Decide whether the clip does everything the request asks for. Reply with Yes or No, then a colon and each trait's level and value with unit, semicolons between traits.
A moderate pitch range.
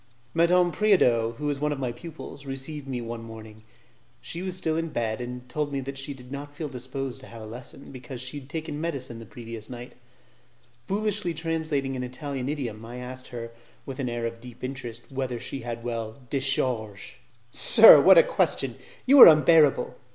Yes: average, 3.9 semitones